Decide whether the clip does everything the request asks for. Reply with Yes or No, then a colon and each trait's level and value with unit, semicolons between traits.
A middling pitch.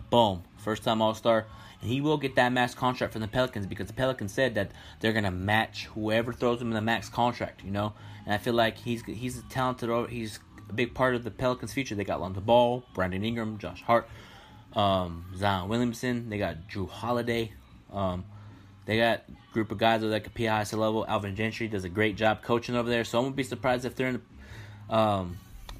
No: low, 110 Hz